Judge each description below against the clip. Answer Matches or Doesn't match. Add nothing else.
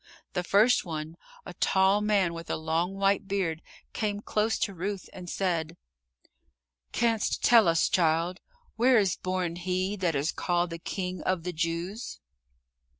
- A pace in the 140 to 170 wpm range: Matches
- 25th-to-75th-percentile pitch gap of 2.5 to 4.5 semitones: Matches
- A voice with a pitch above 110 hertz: Matches